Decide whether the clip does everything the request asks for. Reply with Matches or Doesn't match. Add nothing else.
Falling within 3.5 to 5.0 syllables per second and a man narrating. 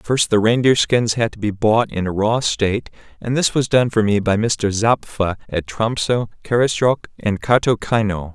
Matches